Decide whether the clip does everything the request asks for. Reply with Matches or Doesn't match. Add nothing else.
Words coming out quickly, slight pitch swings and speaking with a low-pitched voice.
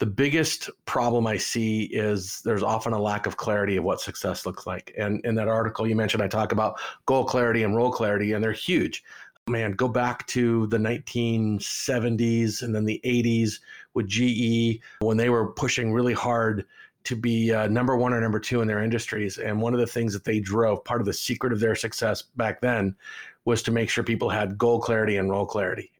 Matches